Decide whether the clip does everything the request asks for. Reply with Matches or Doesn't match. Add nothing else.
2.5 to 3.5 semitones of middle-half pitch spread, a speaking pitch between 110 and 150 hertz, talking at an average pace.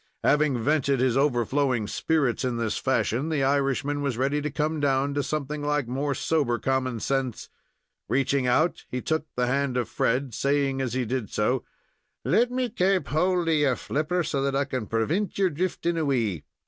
Matches